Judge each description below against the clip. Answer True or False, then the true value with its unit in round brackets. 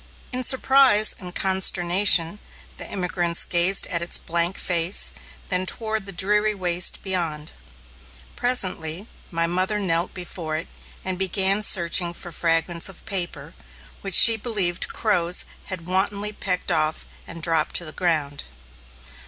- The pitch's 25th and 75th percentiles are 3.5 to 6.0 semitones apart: False (2.8 semitones)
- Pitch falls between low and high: True (180 Hz)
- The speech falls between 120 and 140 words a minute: True (135 wpm)